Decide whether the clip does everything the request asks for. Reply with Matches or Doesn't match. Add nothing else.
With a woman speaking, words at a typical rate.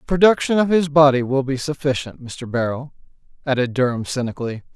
Doesn't match